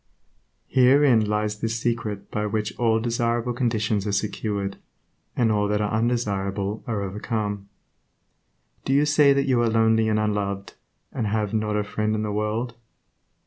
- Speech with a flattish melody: Yes, narrow, 2.1 semitones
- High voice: No, low, 110 Hz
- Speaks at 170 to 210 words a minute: No, average, 155 wpm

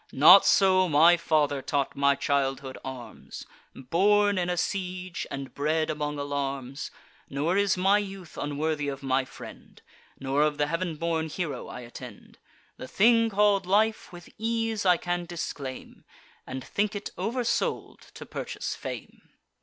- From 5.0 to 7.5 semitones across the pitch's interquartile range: Yes, wide, 5.5 semitones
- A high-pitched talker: No, medium, 165 Hz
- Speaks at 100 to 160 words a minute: Yes, average, 150 wpm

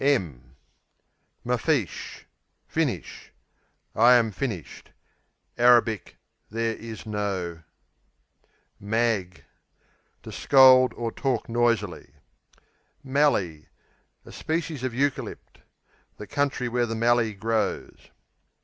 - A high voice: No, low, 115 Hz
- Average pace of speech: No, slow, 85 wpm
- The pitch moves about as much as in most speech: Yes, average, 3.2 semitones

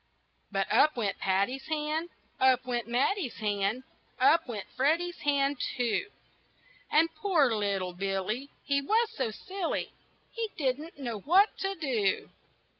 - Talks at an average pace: No, slow, 130 wpm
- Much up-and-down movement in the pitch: Yes, wide, 7.0 semitones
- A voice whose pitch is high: Yes, very high, 265 Hz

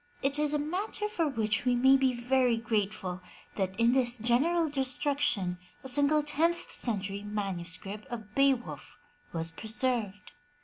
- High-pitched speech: Yes, high, 240 Hz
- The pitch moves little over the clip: No, average, 5.2 semitones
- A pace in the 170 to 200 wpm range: No, average, 140 wpm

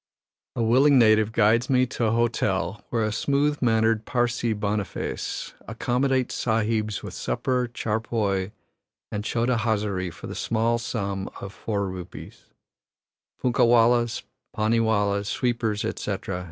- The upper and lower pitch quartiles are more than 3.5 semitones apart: No, narrow, 2.5 semitones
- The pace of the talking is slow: Yes, slow, 125 wpm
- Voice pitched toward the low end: Yes, low, 115 Hz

